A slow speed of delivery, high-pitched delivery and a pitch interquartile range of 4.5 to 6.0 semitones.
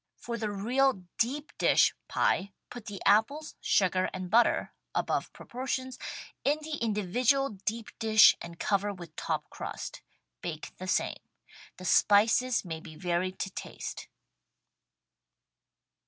Yes: slow, 125 wpm; high, 210 Hz; average, 4.9 semitones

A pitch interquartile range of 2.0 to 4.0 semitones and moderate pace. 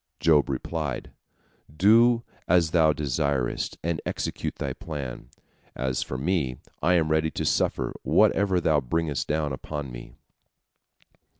No: average, 3.4 semitones; slow, 125 wpm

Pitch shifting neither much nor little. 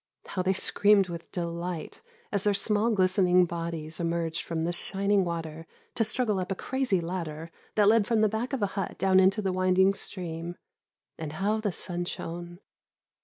Yes: average, 3.1 semitones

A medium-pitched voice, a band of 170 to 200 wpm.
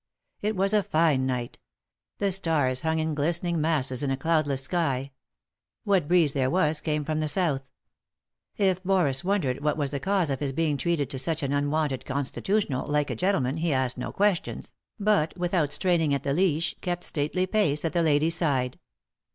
Yes: medium, 155 Hz; average, 185 wpm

